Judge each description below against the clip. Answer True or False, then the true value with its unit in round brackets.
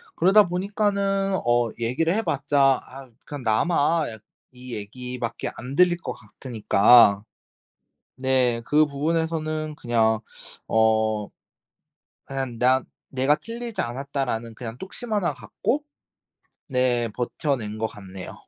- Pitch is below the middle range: True (130 Hz)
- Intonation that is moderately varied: False (5.8 semitones)